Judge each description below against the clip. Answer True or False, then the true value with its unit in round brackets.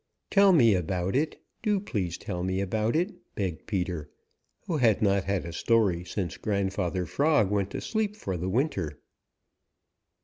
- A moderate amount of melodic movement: False (6.1 semitones)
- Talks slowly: False (160 wpm)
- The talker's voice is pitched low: True (100 Hz)